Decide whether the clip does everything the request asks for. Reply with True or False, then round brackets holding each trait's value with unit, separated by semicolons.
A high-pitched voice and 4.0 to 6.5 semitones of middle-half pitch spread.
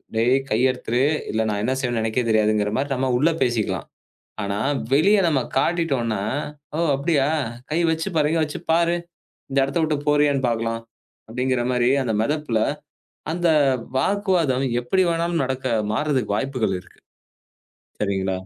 False (130 Hz; 5.0 semitones)